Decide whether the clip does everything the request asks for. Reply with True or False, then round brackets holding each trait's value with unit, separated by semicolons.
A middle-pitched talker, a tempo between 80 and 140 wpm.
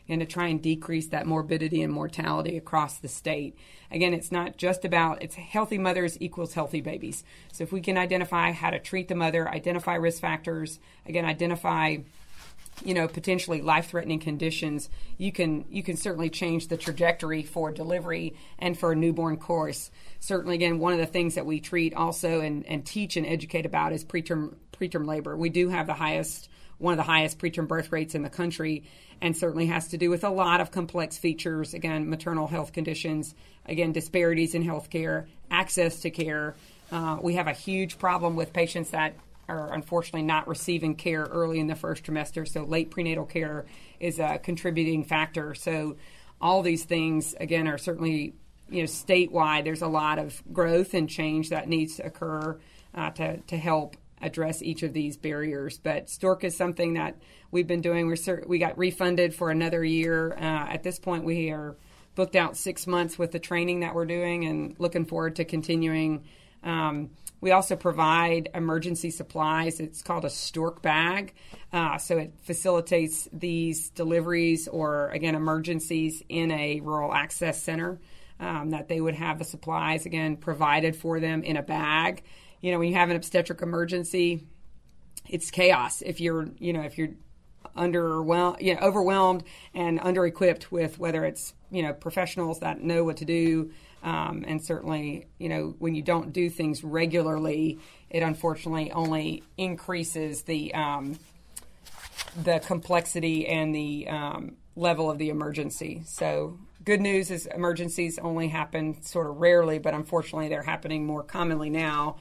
False (165 Hz; 175 wpm)